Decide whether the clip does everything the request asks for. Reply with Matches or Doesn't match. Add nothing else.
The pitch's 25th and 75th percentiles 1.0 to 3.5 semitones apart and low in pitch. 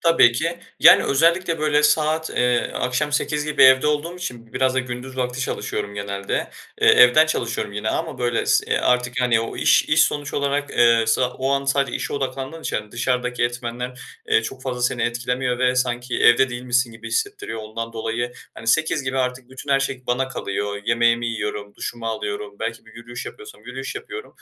Matches